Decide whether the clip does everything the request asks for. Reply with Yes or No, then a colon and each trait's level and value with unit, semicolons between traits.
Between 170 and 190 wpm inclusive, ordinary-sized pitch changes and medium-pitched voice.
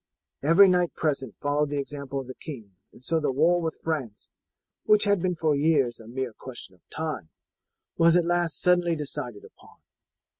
Yes: average, 180 wpm; average, 4.4 semitones; medium, 150 Hz